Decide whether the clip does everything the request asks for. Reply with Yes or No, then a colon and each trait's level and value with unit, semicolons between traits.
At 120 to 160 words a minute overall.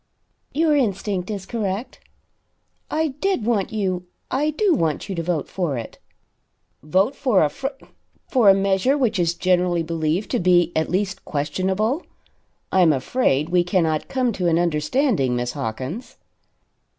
Yes: average, 150 wpm